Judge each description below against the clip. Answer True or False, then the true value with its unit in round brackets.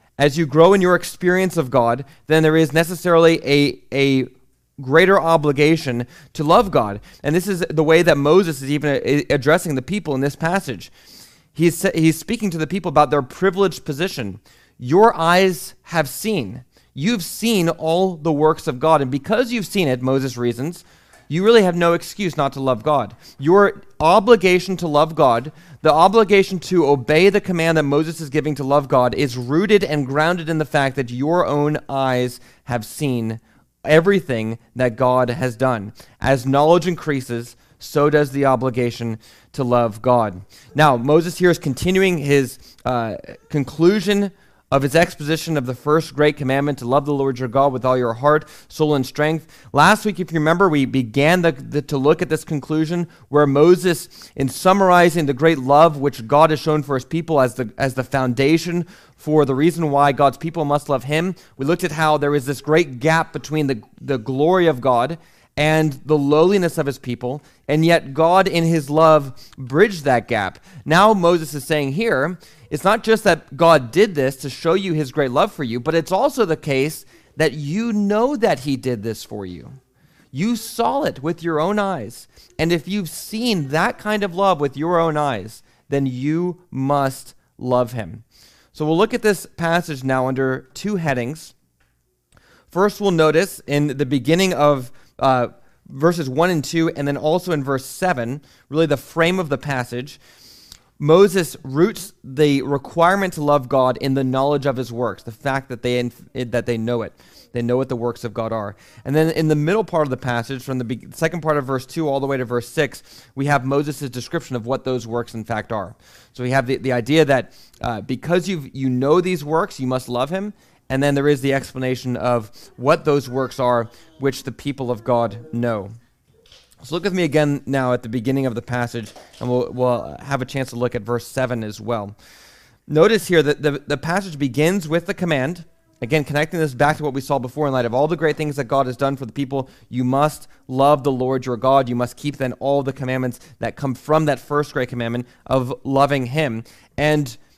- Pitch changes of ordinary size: True (4.2 semitones)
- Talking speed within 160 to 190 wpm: False (200 wpm)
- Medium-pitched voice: True (145 Hz)